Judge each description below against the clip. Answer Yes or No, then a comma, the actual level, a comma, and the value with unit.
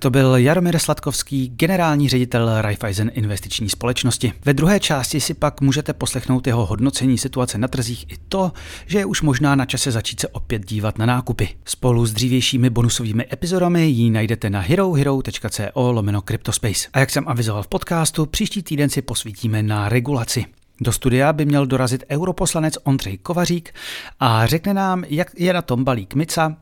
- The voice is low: Yes, low, 130 Hz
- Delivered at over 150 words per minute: Yes, fast, 170 wpm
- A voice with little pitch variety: No, average, 4.8 semitones